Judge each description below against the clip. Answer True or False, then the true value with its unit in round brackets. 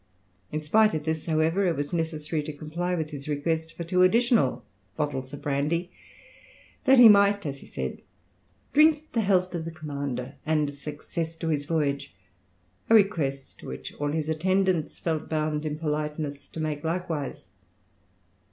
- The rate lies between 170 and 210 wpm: False (160 wpm)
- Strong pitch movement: False (3.3 semitones)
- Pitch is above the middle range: False (155 Hz)